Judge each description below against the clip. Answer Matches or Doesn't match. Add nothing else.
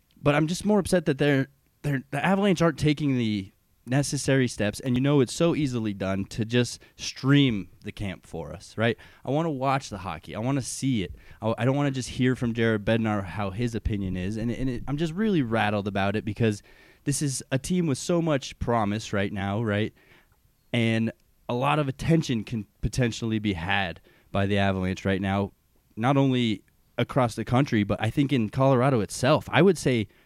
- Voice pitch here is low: Matches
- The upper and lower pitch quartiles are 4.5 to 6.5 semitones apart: Matches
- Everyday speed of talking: Doesn't match